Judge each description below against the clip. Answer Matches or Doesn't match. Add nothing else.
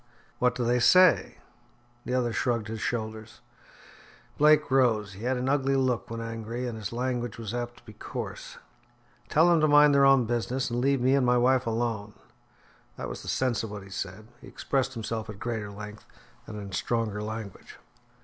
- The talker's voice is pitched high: Doesn't match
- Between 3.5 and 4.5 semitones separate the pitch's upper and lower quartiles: Doesn't match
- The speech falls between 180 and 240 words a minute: Matches